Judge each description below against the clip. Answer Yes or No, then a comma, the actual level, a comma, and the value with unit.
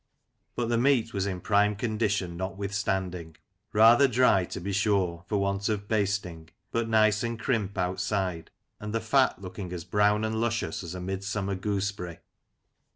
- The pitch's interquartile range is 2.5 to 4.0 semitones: Yes, average, 2.8 semitones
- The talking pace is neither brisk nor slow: Yes, average, 155 wpm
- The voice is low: Yes, low, 100 Hz